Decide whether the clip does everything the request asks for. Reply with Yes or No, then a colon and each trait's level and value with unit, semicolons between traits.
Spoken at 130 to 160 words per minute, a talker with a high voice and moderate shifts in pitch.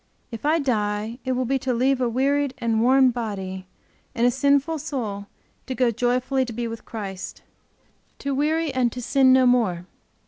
No: average, 180 wpm; very high, 250 Hz; average, 3.0 semitones